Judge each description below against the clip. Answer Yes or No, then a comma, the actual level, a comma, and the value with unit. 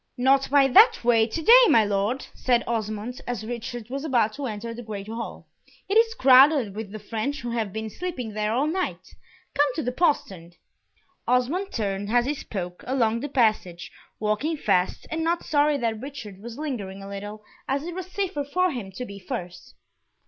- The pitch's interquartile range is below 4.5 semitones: No, average, 5.2 semitones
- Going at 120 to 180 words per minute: No, average, 190 wpm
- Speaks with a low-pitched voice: No, high, 240 Hz